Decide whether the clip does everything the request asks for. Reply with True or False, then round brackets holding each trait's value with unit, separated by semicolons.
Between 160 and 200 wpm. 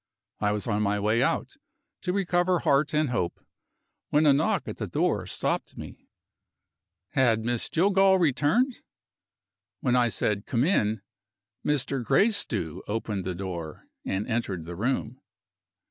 False (140 wpm)